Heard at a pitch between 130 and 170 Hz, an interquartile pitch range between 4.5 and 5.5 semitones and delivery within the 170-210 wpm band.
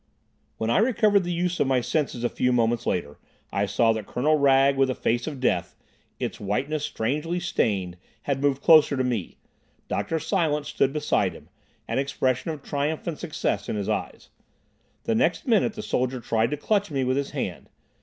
Yes: medium, 140 Hz; average, 5.0 semitones; average, 190 wpm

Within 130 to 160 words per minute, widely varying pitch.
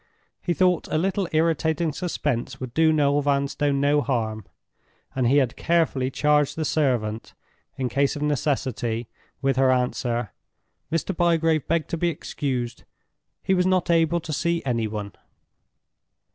No: average, 145 wpm; average, 4.3 semitones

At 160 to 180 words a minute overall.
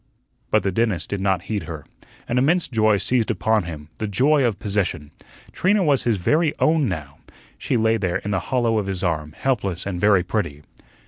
No: average, 195 wpm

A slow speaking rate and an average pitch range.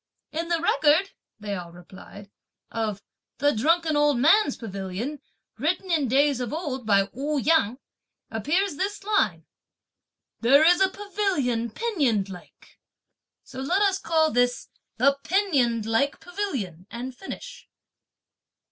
No: slow, 130 wpm; wide, 7.3 semitones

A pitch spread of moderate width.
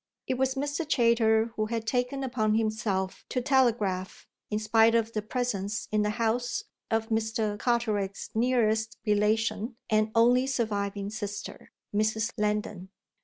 No: narrow, 2.2 semitones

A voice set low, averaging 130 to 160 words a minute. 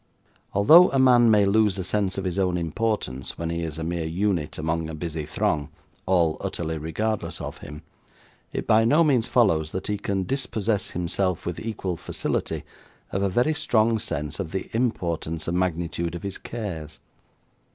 No: very low, 95 Hz; average, 175 wpm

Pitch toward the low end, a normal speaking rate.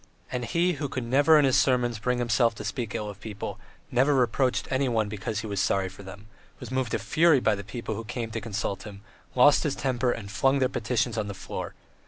No: low, 120 Hz; fast, 235 wpm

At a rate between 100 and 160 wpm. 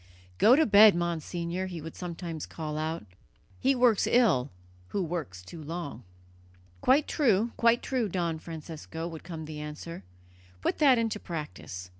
Yes: average, 150 wpm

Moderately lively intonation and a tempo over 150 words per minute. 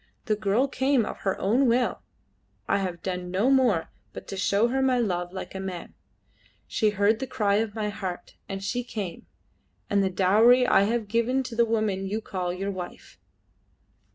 Yes: average, 3.6 semitones; average, 185 wpm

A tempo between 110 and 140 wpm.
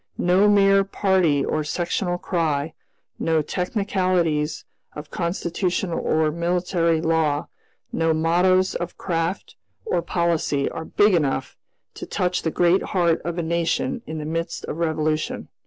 Yes: slow, 135 wpm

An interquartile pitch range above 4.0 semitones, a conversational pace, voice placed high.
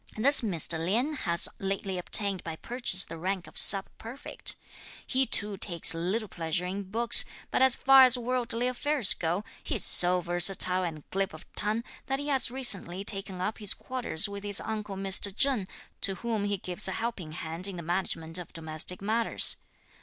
Yes: average, 4.6 semitones; average, 185 wpm; high, 195 Hz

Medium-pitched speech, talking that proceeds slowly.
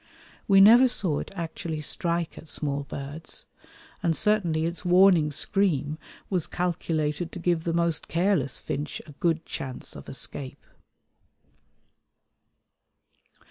Yes: medium, 165 Hz; slow, 120 wpm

